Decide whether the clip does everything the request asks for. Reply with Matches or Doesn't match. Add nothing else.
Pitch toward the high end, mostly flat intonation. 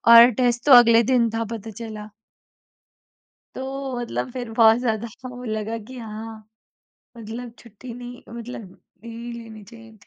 Matches